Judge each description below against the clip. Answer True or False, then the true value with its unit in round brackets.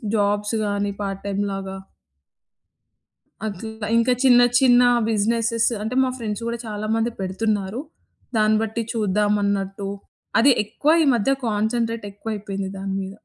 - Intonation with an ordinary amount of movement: False (2.3 semitones)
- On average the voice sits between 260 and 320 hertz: False (210 Hz)